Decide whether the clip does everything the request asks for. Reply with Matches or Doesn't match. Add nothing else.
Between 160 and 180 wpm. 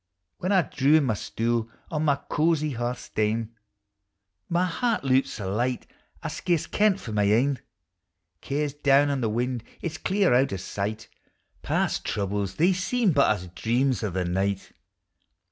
Matches